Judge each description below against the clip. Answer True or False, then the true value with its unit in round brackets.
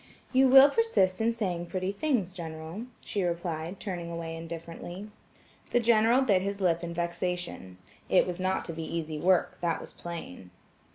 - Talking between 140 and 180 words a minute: True (165 wpm)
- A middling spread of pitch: True (3.3 semitones)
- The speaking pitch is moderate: True (180 Hz)